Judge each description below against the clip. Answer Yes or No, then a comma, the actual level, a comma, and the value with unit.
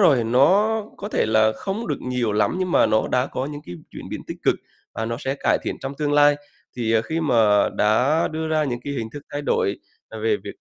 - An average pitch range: No, wide, 5.8 semitones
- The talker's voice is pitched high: No, medium, 140 Hz